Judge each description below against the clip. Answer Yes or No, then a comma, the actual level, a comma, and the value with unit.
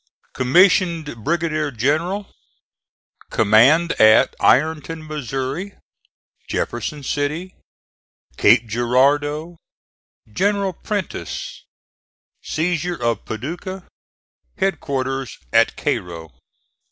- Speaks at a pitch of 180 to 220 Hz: No, medium, 150 Hz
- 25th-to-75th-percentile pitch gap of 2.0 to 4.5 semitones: No, average, 5.3 semitones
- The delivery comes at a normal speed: No, slow, 65 wpm